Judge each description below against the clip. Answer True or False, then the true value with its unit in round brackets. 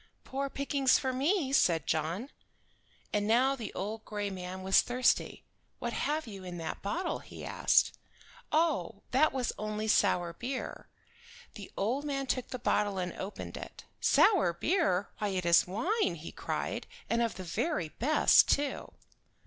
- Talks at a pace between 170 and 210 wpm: False (155 wpm)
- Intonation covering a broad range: True (6.6 semitones)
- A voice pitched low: False (220 Hz)